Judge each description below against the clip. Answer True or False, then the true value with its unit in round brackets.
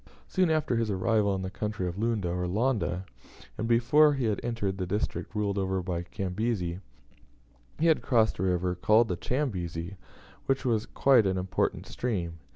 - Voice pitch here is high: False (105 Hz)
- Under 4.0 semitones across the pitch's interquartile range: False (4.3 semitones)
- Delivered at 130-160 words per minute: False (170 wpm)